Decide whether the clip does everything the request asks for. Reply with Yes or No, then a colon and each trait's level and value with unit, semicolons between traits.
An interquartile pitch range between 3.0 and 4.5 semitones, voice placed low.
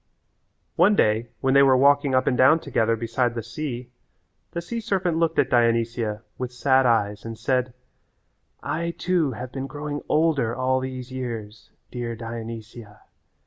Yes: average, 3.5 semitones; low, 125 Hz